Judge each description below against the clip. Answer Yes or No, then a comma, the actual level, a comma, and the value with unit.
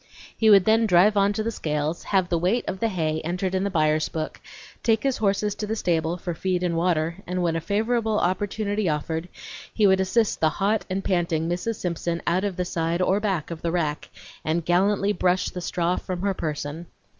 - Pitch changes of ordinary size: Yes, average, 3.3 semitones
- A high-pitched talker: No, medium, 180 Hz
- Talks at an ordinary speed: No, fast, 215 wpm